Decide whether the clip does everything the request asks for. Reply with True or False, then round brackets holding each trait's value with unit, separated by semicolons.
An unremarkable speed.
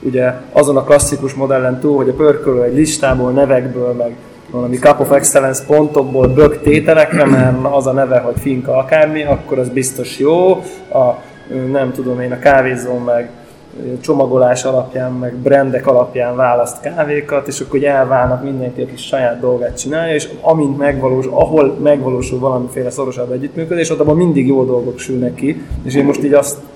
False (170 wpm)